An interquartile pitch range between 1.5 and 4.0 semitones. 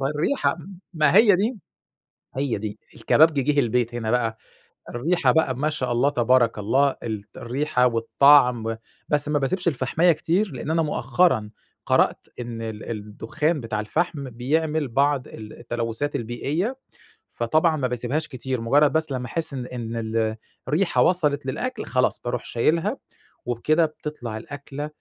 No: average, 4.8 semitones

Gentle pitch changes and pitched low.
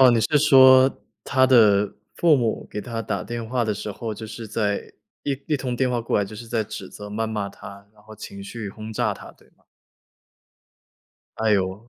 No: average, 3.1 semitones; low, 110 Hz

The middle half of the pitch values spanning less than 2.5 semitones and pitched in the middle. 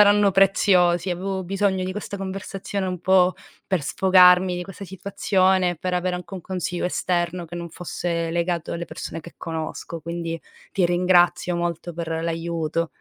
Yes: narrow, 1.8 semitones; medium, 180 Hz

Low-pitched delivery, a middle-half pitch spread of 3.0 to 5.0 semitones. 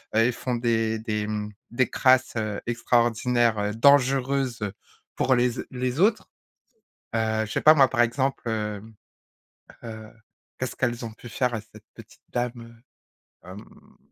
No: low, 120 Hz; narrow, 2.5 semitones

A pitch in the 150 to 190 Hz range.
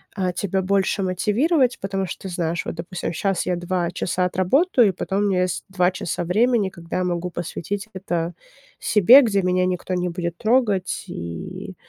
Yes: medium, 185 Hz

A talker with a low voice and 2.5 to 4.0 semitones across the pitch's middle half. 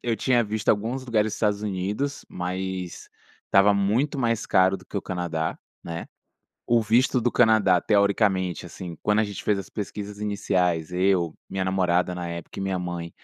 Yes: low, 100 Hz; average, 3.1 semitones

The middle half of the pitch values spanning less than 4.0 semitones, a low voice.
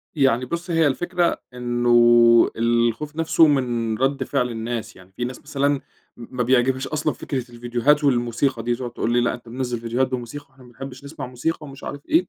Yes: average, 2.9 semitones; low, 125 Hz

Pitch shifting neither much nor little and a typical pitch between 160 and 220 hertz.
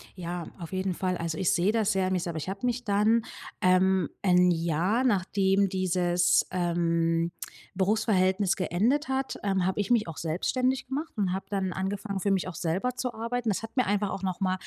Yes: average, 3.1 semitones; high, 190 Hz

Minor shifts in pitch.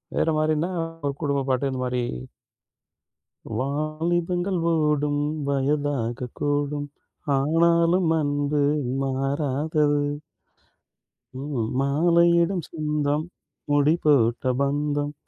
Yes: narrow, 2.1 semitones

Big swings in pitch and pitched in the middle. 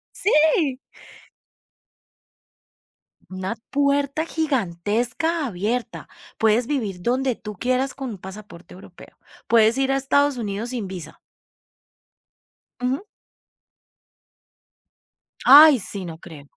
No: wide, 6.0 semitones; high, 240 Hz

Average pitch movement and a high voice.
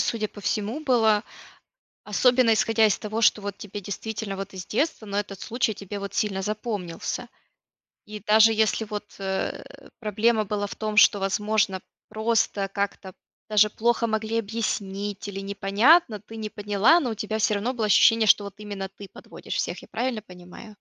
No: narrow, 1.8 semitones; high, 210 Hz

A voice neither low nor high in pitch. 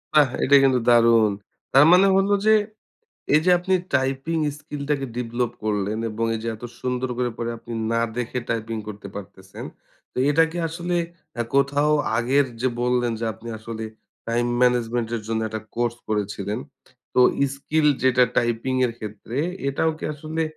No: low, 120 Hz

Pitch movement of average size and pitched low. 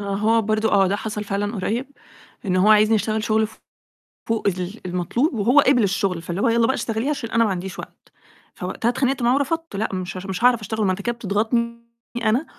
No: average, 3.0 semitones; high, 220 Hz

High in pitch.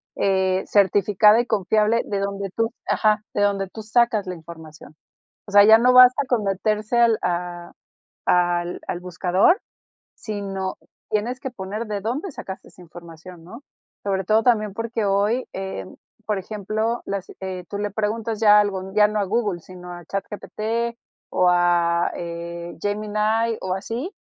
Yes: high, 205 Hz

